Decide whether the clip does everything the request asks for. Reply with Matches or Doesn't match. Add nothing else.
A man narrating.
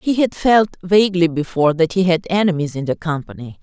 Doesn't match